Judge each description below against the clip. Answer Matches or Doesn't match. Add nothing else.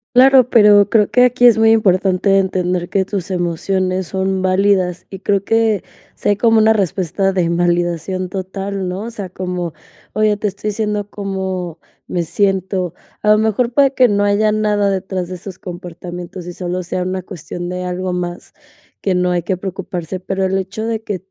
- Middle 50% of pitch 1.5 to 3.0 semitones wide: Matches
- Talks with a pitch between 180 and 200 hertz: Matches